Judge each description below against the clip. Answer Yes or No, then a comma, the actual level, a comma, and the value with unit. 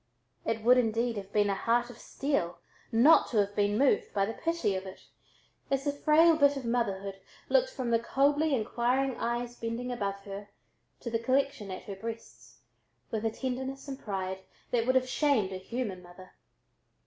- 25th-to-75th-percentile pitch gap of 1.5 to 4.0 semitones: No, average, 4.8 semitones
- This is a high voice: Yes, high, 230 Hz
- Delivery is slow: No, average, 185 wpm